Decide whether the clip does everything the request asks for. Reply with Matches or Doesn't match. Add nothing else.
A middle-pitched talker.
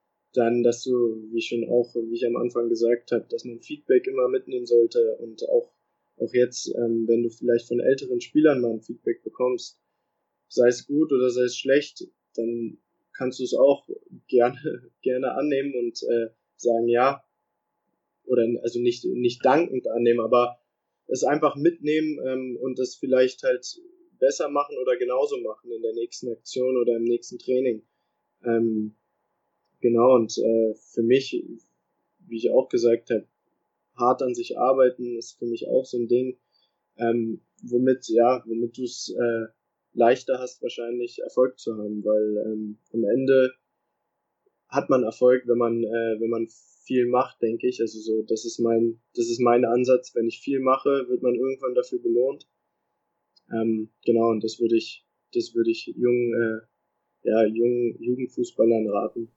Doesn't match